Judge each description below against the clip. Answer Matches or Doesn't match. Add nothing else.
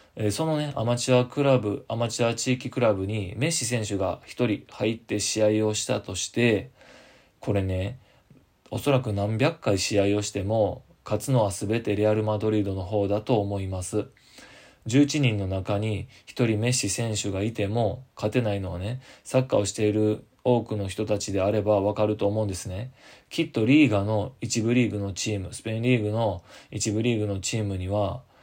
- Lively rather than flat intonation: Doesn't match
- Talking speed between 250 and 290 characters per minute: Doesn't match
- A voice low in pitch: Matches